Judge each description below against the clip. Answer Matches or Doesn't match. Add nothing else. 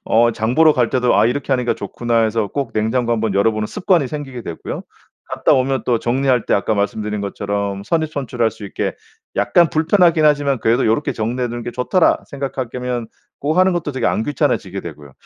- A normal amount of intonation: Matches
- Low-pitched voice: Matches